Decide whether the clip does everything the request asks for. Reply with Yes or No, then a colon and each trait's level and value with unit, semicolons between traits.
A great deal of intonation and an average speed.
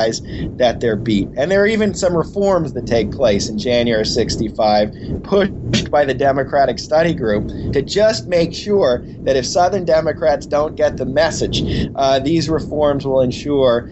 Yes: wide, 5.9 semitones; average, 165 wpm